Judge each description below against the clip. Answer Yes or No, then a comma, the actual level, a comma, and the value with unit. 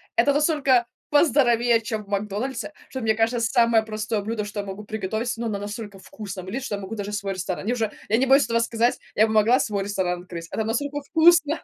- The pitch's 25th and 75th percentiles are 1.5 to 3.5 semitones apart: Yes, average, 3.1 semitones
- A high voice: Yes, high, 220 Hz